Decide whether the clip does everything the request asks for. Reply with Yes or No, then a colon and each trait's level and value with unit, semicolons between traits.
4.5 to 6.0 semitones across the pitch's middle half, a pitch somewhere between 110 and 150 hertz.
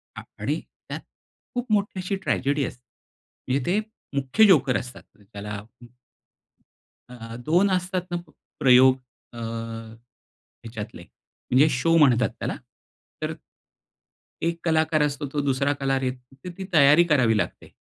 Yes: average, 5.1 semitones; low, 135 Hz